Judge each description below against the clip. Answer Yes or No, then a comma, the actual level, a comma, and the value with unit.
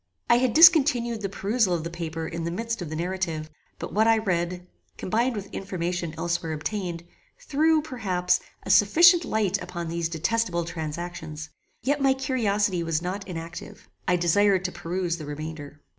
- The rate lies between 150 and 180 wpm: Yes, average, 165 wpm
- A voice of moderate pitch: Yes, medium, 180 Hz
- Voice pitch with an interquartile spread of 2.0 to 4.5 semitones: No, average, 5.0 semitones